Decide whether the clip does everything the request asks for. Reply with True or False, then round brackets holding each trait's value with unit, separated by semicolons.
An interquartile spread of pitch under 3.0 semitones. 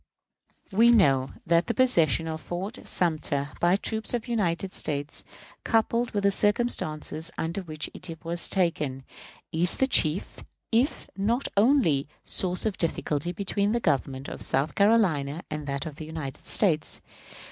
False (5.4 semitones)